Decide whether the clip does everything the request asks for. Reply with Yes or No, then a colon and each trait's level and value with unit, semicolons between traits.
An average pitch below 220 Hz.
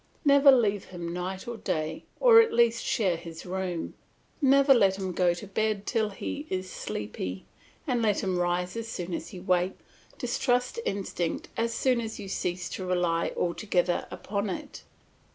Yes: high, 190 Hz